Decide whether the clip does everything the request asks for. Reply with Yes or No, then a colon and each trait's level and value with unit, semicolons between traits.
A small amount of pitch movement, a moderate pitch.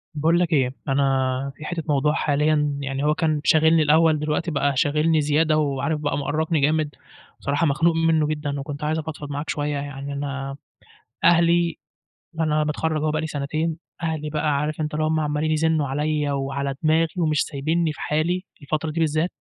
Yes: narrow, 1.9 semitones; medium, 150 Hz